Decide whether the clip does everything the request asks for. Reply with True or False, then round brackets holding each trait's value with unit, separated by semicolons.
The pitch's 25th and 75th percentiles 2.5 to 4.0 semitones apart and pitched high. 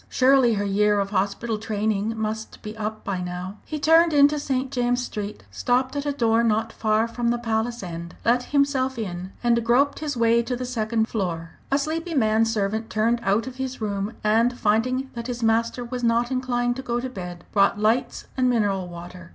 True (3.1 semitones; 230 Hz)